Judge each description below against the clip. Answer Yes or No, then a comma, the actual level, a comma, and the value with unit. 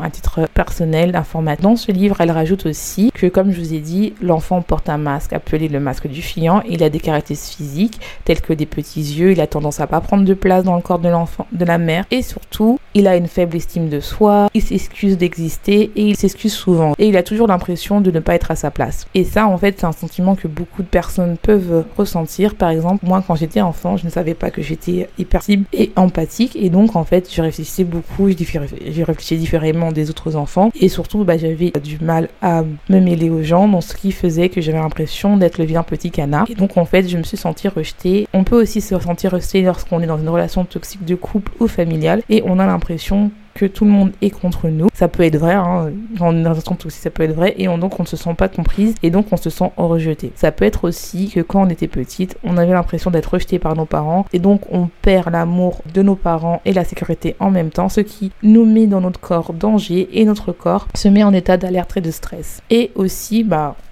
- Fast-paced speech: Yes, fast, 245 wpm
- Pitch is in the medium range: Yes, medium, 180 Hz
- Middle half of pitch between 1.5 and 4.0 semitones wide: Yes, average, 3.0 semitones